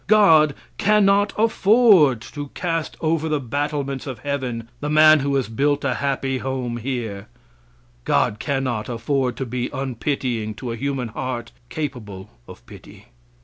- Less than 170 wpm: Yes, average, 145 wpm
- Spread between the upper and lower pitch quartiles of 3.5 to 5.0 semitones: Yes, average, 4.0 semitones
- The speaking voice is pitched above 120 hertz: Yes, low, 135 Hz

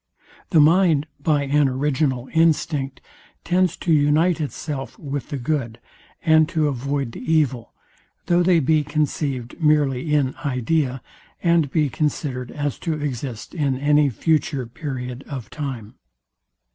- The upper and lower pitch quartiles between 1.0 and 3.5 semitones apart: Yes, average, 3.0 semitones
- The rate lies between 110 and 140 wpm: Yes, slow, 135 wpm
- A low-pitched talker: No, medium, 145 Hz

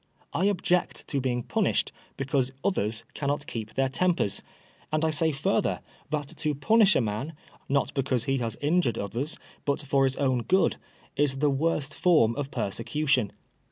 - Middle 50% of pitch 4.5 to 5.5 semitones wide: No, average, 3.5 semitones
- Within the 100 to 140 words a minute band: No, average, 160 wpm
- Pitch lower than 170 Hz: Yes, medium, 140 Hz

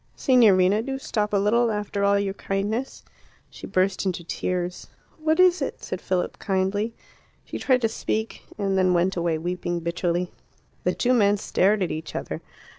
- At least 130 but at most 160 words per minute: No, average, 170 wpm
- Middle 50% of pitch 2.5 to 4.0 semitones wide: Yes, average, 3.4 semitones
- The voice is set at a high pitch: Yes, high, 200 Hz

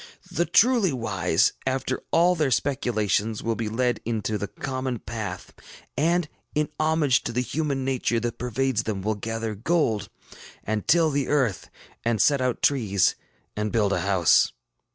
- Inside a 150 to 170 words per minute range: Yes, average, 155 wpm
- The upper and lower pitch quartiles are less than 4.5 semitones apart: No, average, 4.9 semitones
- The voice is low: Yes, low, 120 Hz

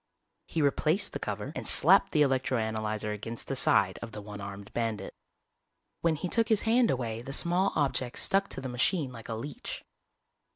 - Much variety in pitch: Yes, wide, 6.5 semitones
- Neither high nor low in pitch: No, low, 130 Hz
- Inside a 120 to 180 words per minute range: No, average, 190 wpm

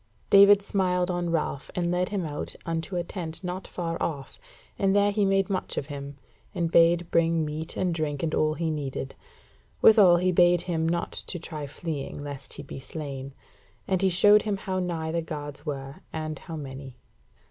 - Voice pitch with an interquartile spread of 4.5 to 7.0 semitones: No, average, 3.4 semitones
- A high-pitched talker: No, medium, 165 Hz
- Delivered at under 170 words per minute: No, average, 190 wpm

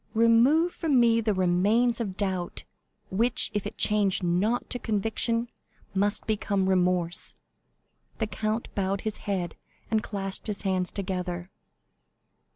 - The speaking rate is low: Yes, slow, 130 wpm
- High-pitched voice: Yes, high, 205 Hz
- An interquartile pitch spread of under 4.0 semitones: Yes, average, 3.4 semitones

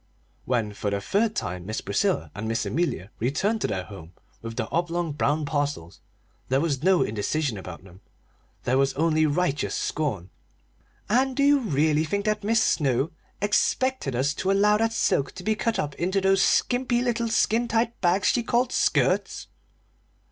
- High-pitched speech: No, medium, 155 Hz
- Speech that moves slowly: No, average, 170 wpm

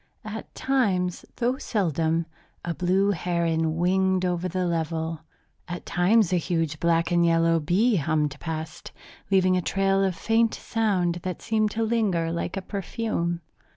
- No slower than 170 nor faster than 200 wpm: No, average, 150 wpm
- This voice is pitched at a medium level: Yes, medium, 180 Hz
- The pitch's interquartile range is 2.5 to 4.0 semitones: Yes, average, 3.0 semitones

